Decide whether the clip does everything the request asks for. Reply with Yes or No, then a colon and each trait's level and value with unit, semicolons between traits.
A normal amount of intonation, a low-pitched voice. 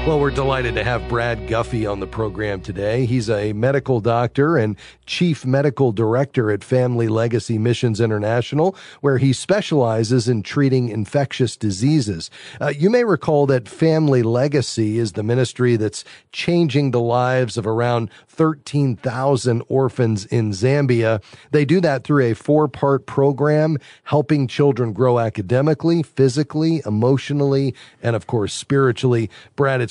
Yes: average, 3.8 semitones; low, 125 Hz